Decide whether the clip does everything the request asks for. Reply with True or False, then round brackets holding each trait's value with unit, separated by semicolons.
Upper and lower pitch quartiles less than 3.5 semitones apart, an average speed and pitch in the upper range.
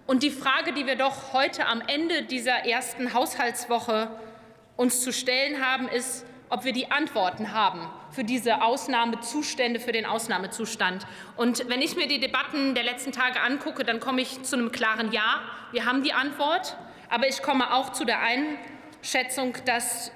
True (2.4 semitones; 170 wpm; 250 Hz)